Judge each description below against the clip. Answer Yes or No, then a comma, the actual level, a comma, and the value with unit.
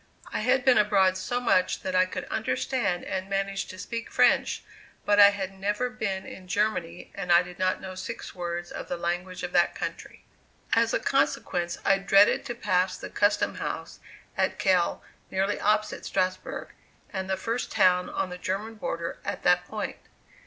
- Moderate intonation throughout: No, narrow, 2.3 semitones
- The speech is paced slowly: No, average, 180 wpm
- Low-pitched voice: No, high, 190 Hz